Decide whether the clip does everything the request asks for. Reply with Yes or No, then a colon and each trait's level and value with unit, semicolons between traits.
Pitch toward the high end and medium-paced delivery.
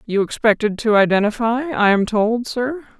Yes: high, 225 Hz; average, 160 wpm